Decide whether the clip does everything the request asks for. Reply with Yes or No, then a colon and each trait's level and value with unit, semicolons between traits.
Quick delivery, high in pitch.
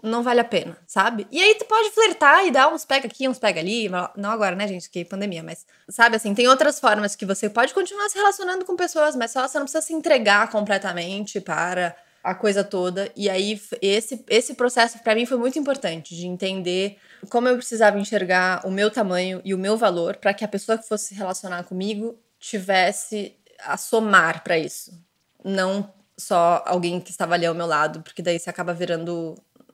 Yes: fast, 205 wpm; high, 205 Hz